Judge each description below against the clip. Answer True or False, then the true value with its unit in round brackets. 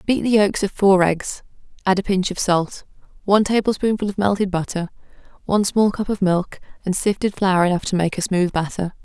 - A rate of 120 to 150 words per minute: False (200 wpm)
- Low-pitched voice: False (190 Hz)